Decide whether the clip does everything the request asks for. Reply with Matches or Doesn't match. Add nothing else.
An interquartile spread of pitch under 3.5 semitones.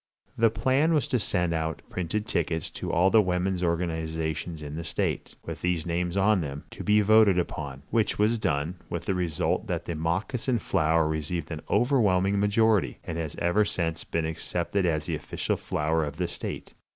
Doesn't match